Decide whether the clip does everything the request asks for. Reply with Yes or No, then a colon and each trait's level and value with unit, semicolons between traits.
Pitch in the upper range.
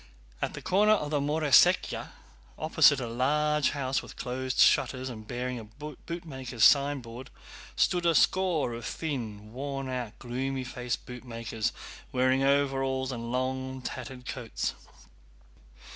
No: low, 130 Hz